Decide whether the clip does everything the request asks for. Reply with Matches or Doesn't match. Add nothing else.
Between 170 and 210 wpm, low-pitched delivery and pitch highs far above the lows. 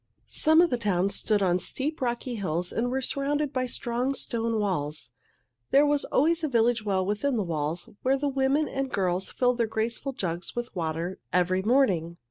Doesn't match